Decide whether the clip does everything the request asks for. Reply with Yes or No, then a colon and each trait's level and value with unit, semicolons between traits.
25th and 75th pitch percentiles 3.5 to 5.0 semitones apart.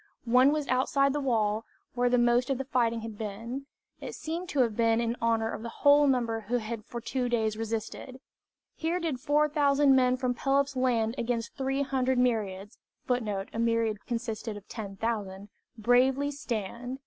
No: average, 3.1 semitones